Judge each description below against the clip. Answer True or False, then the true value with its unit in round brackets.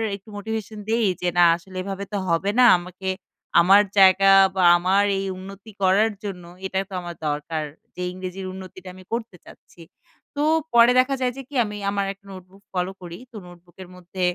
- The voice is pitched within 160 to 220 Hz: True (190 Hz)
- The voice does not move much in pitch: True (2.1 semitones)